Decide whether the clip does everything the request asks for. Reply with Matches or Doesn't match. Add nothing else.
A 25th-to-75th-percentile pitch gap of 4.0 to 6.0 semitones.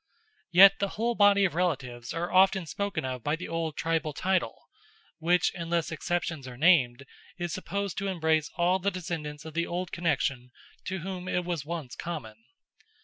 Doesn't match